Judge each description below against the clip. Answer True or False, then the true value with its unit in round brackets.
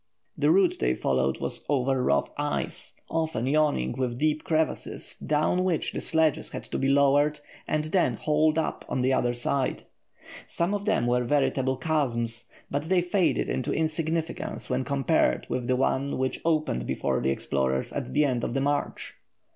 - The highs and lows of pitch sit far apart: False (3.9 semitones)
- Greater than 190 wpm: False (170 wpm)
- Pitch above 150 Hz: False (140 Hz)